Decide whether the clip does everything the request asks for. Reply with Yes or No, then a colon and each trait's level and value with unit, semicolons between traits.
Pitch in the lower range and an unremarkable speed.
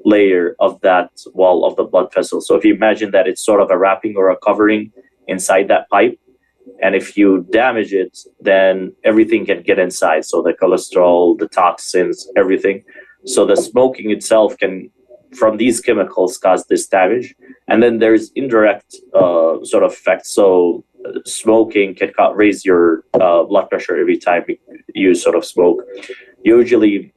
No: very high, 285 Hz; average, 165 wpm